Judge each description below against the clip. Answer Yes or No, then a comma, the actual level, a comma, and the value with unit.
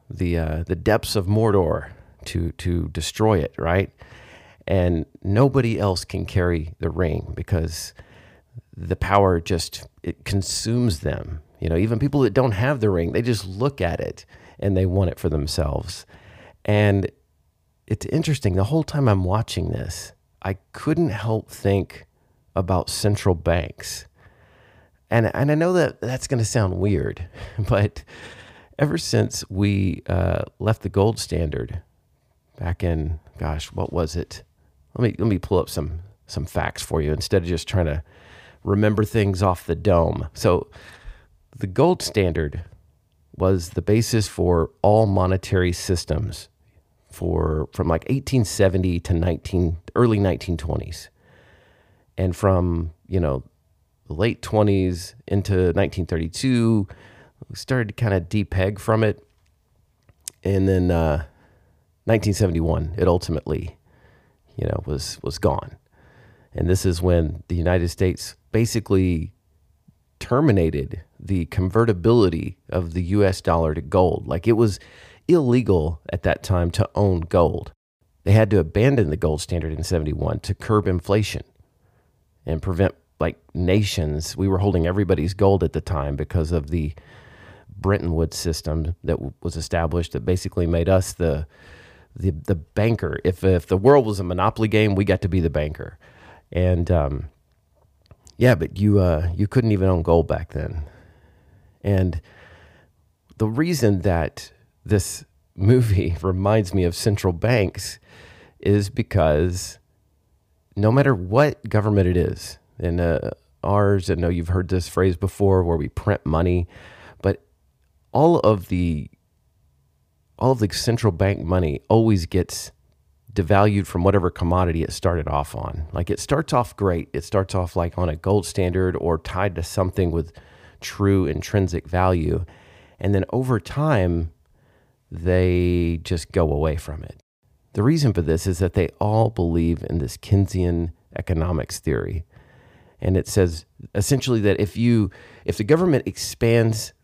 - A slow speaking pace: No, average, 145 wpm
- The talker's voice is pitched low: Yes, very low, 95 Hz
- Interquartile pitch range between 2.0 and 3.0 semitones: No, average, 3.7 semitones